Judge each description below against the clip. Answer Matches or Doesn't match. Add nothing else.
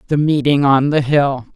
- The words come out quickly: Doesn't match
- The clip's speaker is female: Matches